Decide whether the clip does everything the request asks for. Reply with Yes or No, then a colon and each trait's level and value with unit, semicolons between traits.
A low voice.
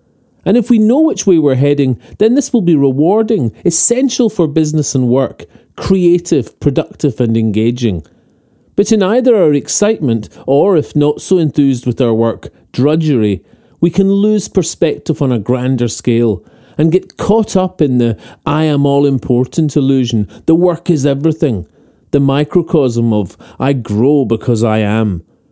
No: medium, 145 Hz